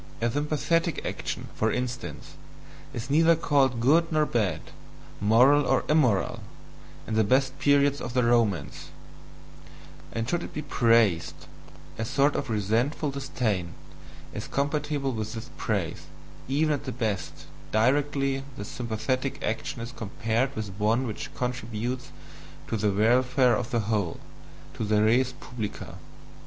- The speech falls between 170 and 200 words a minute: No, slow, 135 wpm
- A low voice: Yes, low, 125 Hz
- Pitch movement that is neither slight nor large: Yes, average, 4.1 semitones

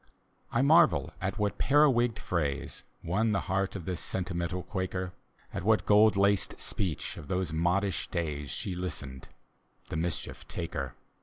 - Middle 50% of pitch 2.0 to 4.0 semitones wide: Yes, average, 3.5 semitones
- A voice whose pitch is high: No, very low, 95 Hz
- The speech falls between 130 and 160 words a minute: Yes, average, 155 wpm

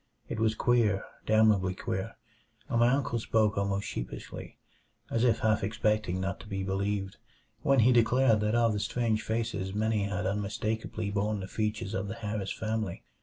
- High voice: No, low, 110 Hz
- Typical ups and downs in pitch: No, narrow, 2.1 semitones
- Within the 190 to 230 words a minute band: No, average, 170 wpm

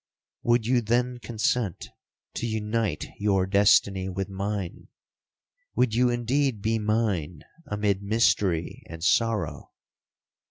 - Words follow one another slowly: Yes, slow, 110 wpm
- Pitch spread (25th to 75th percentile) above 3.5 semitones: No, average, 3.1 semitones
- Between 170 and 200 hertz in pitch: No, low, 105 Hz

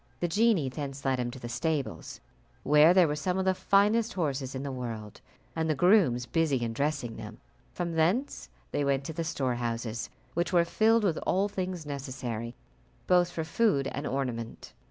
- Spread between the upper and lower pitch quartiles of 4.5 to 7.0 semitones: Yes, wide, 5.6 semitones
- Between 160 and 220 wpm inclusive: Yes, average, 175 wpm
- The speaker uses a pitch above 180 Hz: No, medium, 150 Hz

